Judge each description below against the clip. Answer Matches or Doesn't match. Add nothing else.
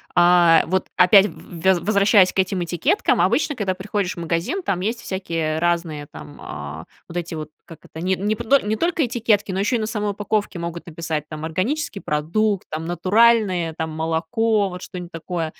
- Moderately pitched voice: Matches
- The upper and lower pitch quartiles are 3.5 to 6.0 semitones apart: Matches